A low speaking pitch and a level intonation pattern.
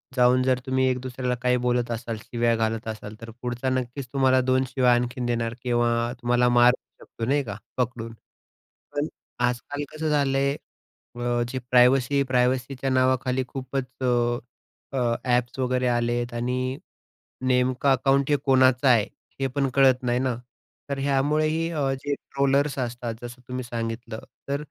Yes: low, 125 Hz; narrow, 1.8 semitones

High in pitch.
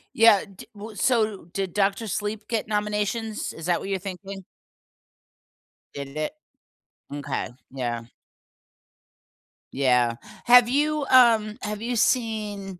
Yes: high, 210 Hz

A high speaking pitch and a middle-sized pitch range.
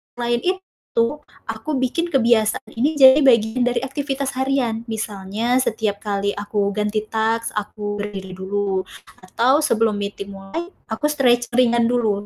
Yes: high, 230 Hz; average, 4.0 semitones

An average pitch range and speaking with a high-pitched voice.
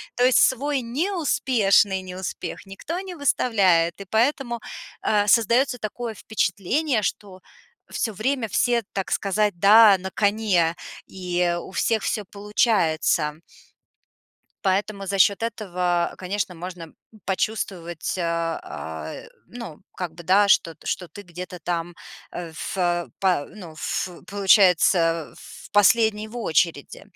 Yes: average, 4.0 semitones; high, 195 Hz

